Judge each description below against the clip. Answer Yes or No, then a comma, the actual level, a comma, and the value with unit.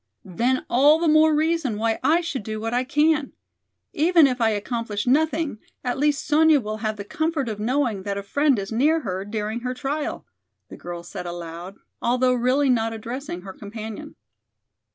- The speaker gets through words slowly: No, average, 180 wpm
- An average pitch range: No, wide, 5.7 semitones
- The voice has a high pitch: Yes, high, 245 Hz